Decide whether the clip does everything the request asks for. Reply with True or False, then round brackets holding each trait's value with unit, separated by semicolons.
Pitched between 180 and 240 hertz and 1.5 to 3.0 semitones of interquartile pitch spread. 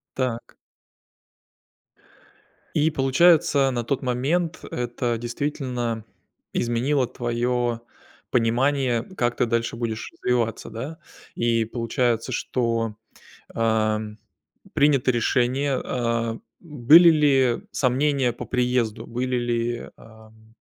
False (120 Hz; 2.5 semitones)